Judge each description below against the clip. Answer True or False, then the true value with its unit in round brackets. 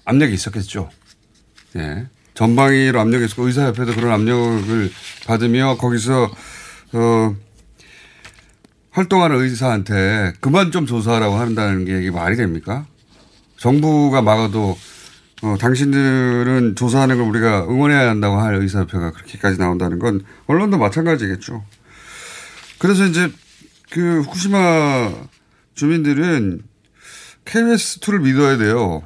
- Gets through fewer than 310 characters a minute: True (285 characters per minute)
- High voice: False (115 Hz)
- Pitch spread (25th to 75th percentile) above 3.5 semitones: True (5.1 semitones)